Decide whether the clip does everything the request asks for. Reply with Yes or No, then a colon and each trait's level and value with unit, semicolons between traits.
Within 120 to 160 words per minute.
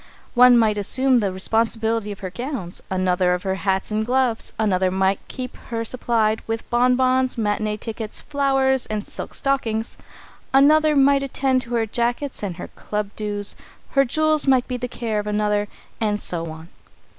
No: average, 170 wpm